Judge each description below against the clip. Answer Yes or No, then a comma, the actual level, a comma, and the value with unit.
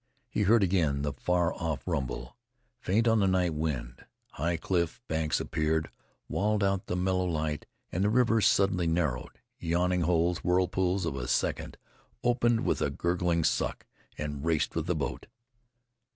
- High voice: No, very low, 90 Hz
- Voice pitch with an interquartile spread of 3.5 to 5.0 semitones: No, average, 3.1 semitones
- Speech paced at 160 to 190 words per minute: No, average, 150 wpm